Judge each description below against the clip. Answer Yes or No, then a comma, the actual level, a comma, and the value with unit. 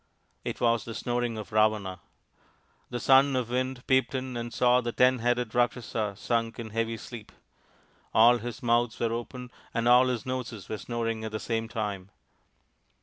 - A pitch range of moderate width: No, narrow, 1.7 semitones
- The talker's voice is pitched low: Yes, low, 120 Hz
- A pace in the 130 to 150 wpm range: No, average, 175 wpm